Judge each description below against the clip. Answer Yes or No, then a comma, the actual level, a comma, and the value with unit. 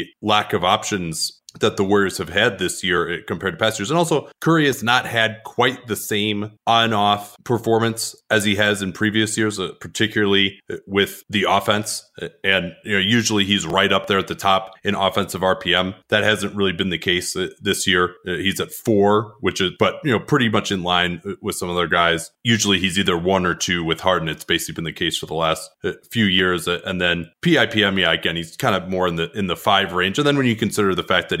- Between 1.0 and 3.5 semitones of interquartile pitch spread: Yes, average, 2.9 semitones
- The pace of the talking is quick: Yes, fast, 225 wpm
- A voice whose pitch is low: Yes, low, 100 Hz